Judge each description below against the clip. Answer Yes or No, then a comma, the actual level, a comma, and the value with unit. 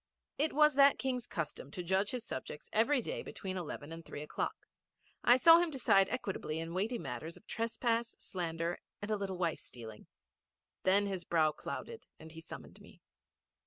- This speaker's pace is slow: No, average, 175 wpm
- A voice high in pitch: Yes, high, 195 Hz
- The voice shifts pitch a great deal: Yes, wide, 6.7 semitones